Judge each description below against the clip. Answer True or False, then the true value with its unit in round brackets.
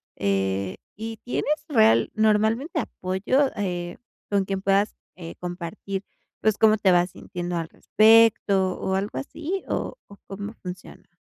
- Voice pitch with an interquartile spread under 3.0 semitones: False (3.6 semitones)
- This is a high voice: True (195 Hz)